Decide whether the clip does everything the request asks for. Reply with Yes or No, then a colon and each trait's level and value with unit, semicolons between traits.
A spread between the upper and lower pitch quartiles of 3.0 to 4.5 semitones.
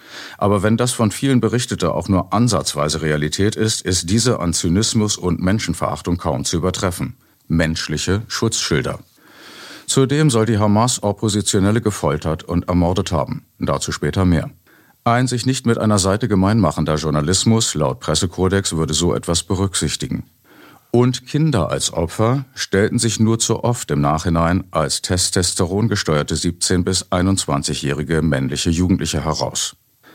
No: average, 5.1 semitones